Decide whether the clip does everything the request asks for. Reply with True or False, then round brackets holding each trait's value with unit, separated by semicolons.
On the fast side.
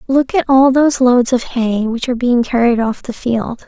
True (230 wpm)